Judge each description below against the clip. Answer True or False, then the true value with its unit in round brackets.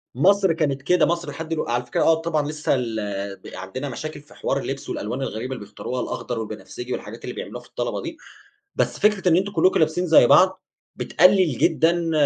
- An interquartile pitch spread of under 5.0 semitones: False (5.6 semitones)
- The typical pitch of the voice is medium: True (150 Hz)